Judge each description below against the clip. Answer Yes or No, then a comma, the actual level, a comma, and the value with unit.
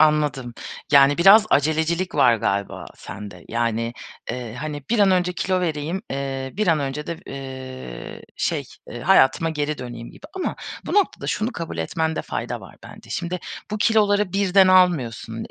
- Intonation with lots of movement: Yes, wide, 5.9 semitones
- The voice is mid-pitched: Yes, medium, 150 Hz